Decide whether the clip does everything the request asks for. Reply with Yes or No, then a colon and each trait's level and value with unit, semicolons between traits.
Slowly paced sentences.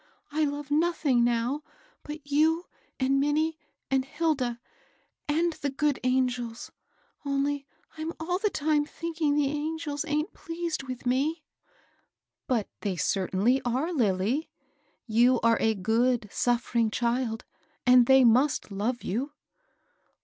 Yes: slow, 125 wpm